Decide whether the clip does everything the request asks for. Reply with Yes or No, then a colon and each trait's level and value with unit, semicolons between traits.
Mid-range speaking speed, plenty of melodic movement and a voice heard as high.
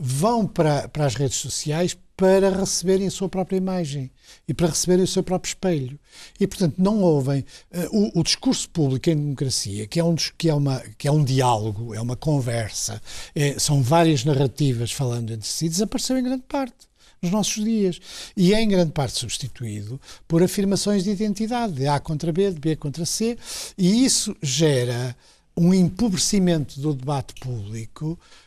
No: average, 175 wpm; wide, 5.9 semitones; medium, 160 Hz